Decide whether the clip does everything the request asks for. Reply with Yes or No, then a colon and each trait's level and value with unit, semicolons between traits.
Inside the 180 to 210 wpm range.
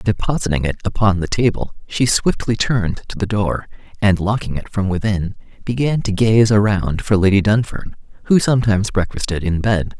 No: average, 170 wpm